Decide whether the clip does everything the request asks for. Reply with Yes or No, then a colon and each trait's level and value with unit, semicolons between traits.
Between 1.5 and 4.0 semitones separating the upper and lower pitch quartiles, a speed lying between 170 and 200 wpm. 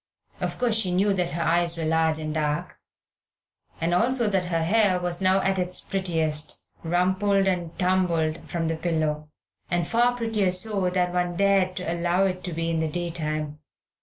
Yes: narrow, 2.6 semitones; average, 175 wpm